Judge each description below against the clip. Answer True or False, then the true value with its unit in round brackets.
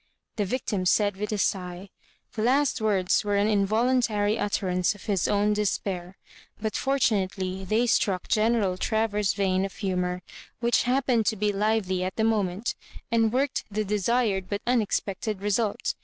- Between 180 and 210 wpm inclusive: False (155 wpm)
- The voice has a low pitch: False (210 Hz)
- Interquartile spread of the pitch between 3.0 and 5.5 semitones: False (2.6 semitones)